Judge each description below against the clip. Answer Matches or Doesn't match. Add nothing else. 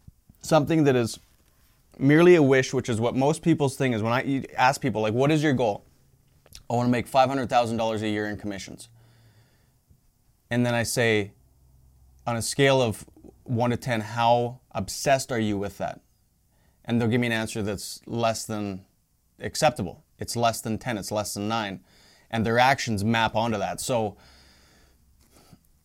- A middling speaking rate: Matches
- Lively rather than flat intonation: Doesn't match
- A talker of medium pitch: Doesn't match